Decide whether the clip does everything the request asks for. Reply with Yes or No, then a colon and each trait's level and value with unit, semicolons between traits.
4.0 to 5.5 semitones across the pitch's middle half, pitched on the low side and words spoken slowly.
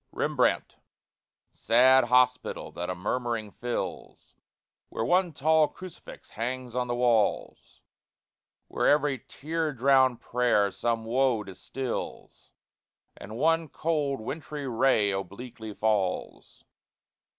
No: average, 3.6 semitones; low, 125 Hz; slow, 105 wpm